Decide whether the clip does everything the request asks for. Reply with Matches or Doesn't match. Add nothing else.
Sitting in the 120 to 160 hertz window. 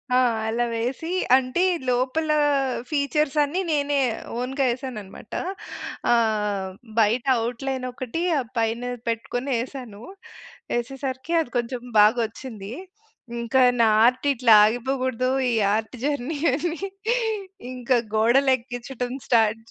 Doesn't match